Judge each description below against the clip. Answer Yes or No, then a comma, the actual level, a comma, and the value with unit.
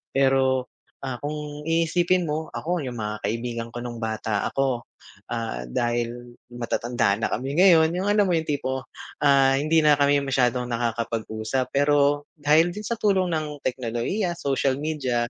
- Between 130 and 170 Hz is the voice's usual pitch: Yes, low, 135 Hz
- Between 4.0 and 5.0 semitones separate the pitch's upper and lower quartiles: Yes, average, 4.5 semitones